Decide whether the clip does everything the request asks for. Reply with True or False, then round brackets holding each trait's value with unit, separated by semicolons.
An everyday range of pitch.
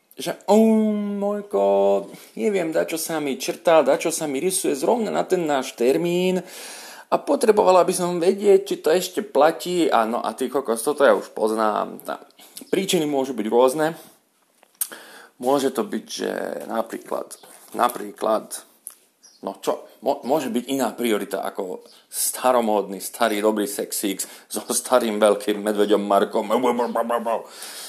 False (8.6 semitones)